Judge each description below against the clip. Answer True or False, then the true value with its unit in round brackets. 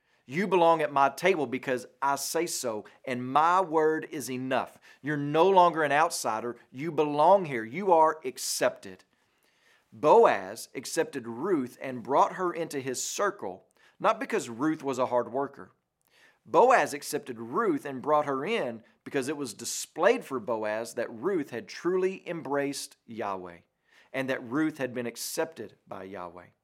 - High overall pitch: False (140 Hz)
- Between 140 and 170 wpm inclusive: True (155 wpm)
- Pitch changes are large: False (4.3 semitones)